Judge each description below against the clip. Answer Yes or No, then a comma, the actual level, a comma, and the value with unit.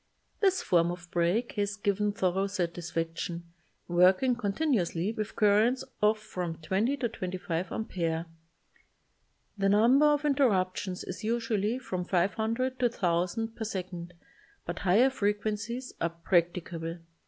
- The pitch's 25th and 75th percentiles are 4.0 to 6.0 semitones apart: Yes, average, 4.5 semitones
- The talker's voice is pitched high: Yes, high, 200 Hz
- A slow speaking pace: Yes, slow, 125 wpm